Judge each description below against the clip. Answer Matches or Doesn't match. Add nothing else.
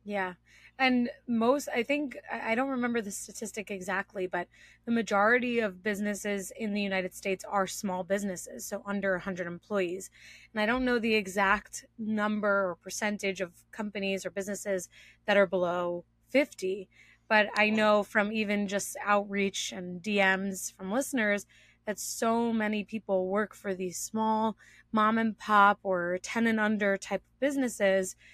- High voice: Matches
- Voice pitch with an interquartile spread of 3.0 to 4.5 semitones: Doesn't match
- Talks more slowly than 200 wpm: Matches